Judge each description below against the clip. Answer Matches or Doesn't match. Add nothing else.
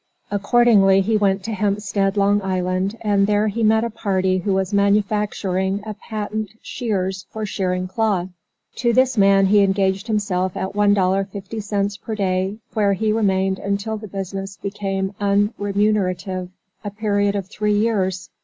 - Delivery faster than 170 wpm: Doesn't match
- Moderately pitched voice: Doesn't match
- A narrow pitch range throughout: Matches